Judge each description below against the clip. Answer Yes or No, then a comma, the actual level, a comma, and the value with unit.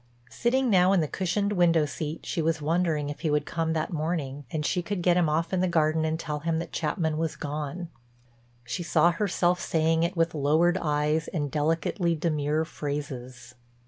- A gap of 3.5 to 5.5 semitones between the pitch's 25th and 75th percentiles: No, narrow, 2.5 semitones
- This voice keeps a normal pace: Yes, average, 190 wpm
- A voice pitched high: No, medium, 160 Hz